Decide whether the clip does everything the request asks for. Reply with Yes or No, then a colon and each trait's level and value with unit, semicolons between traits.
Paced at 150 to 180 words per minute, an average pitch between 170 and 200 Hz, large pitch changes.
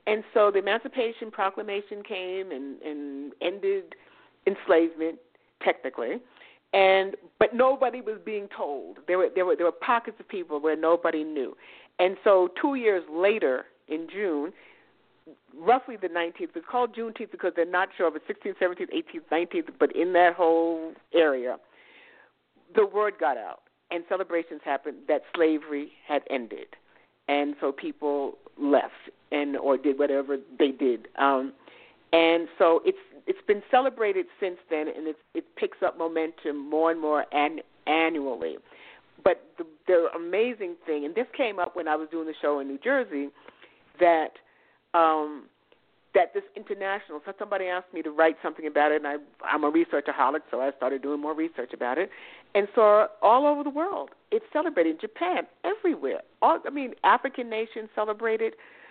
Yes: average, 165 wpm; high, 190 Hz; wide, 8.6 semitones